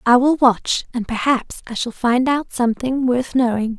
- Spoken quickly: No, average, 190 wpm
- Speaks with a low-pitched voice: No, high, 245 Hz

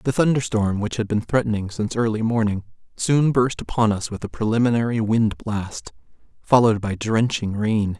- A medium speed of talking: Yes, average, 175 wpm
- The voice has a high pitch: No, low, 110 Hz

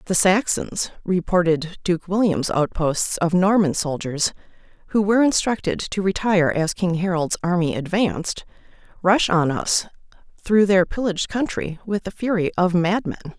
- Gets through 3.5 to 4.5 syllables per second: No, 4.7 syllables/s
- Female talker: Yes, female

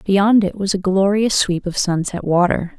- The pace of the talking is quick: No, average, 195 wpm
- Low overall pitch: No, high, 190 Hz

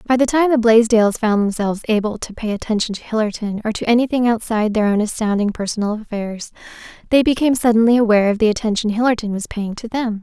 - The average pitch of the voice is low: No, high, 220 Hz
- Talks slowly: No, average, 200 wpm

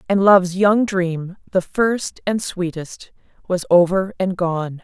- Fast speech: No, average, 150 wpm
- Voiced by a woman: Yes, female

